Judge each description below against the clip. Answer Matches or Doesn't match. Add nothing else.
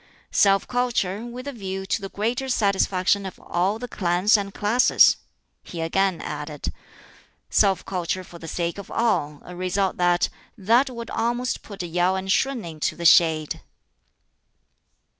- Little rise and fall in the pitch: Doesn't match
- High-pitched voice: Matches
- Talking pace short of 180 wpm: Matches